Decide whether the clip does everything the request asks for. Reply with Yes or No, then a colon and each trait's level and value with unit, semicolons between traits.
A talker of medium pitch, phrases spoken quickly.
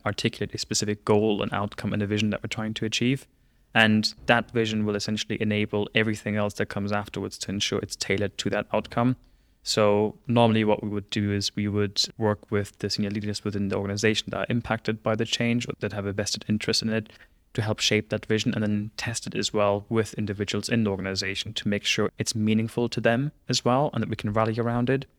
No: low, 105 Hz; fast, 225 wpm